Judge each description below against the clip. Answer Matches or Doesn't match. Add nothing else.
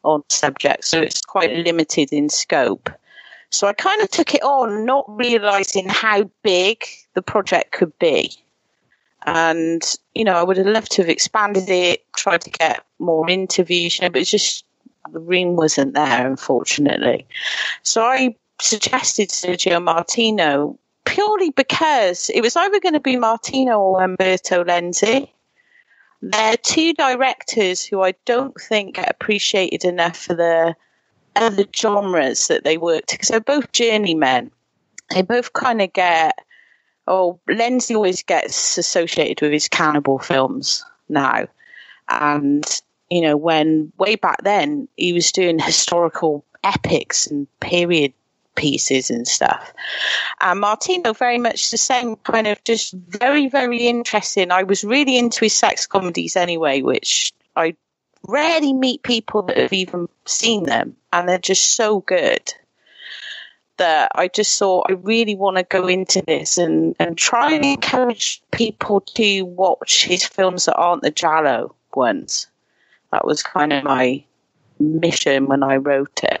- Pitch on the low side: Doesn't match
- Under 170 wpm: Matches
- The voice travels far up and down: Matches